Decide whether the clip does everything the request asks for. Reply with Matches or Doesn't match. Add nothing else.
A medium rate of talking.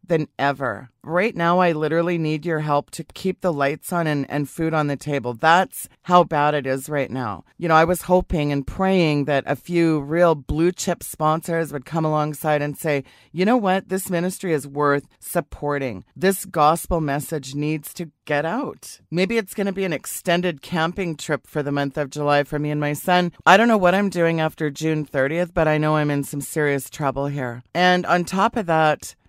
Doesn't match